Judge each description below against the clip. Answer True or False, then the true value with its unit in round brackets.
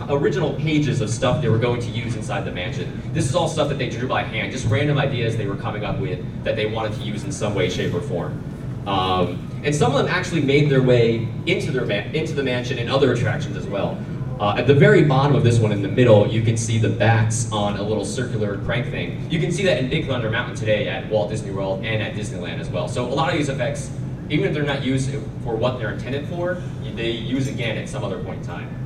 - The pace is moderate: False (260 wpm)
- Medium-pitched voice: False (130 Hz)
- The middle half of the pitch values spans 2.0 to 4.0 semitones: True (3.7 semitones)